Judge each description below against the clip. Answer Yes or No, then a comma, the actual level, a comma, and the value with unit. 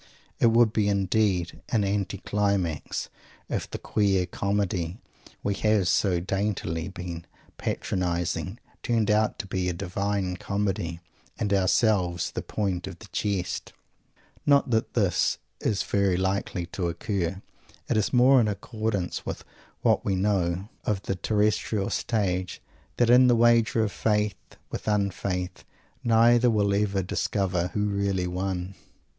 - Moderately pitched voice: No, low, 100 Hz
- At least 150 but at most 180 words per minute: No, average, 140 wpm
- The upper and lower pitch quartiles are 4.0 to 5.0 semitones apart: No, average, 2.7 semitones